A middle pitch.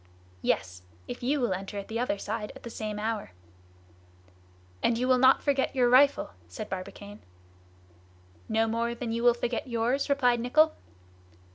No: high, 235 Hz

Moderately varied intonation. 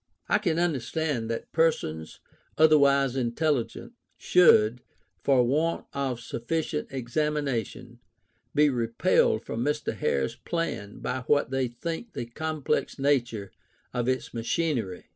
Yes: average, 4.7 semitones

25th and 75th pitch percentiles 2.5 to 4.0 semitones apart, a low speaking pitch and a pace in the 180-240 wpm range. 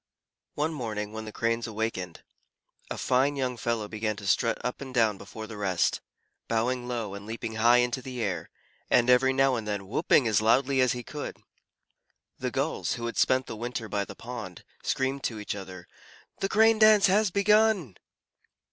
Yes: average, 3.6 semitones; low, 120 Hz; average, 185 wpm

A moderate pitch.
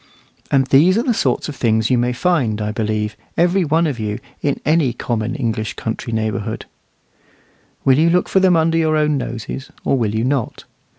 No: low, 130 Hz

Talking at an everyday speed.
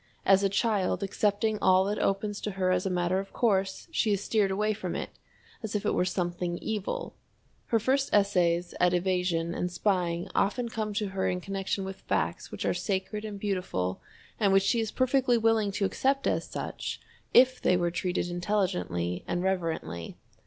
Yes: average, 185 wpm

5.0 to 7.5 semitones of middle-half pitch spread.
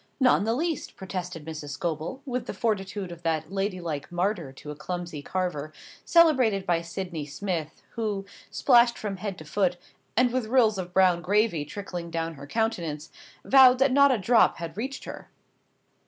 Yes: wide, 5.5 semitones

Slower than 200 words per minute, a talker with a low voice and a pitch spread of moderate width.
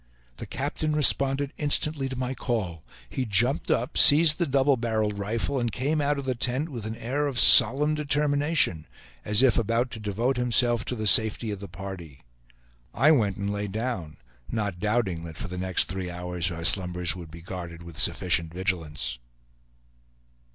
No: average, 175 wpm; low, 110 Hz; wide, 6.7 semitones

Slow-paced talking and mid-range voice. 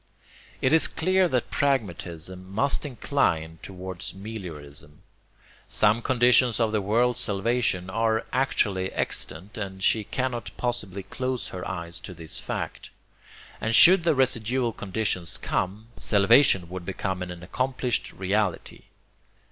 No: slow, 125 wpm; low, 105 Hz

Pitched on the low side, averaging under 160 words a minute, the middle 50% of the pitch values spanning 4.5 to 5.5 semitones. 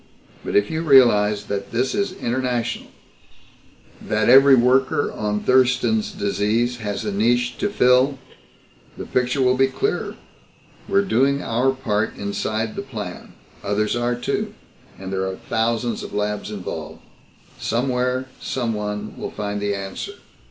No: low, 120 Hz; average, 140 wpm; average, 4.0 semitones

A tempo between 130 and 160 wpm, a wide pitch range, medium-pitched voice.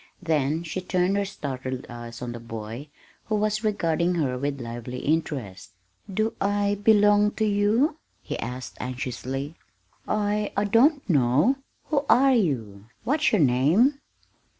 Yes: average, 140 wpm; wide, 8.7 semitones; medium, 170 Hz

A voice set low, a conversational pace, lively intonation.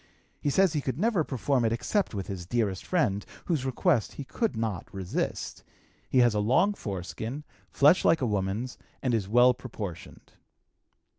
Yes: low, 120 Hz; average, 165 wpm; wide, 5.9 semitones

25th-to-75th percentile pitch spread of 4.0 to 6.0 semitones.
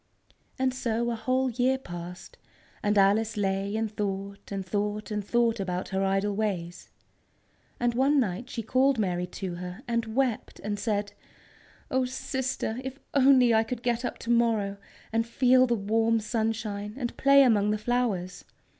No: average, 3.6 semitones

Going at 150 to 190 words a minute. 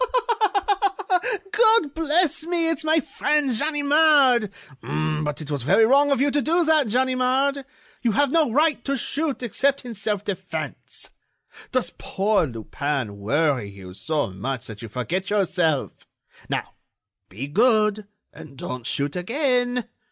No: slow, 135 wpm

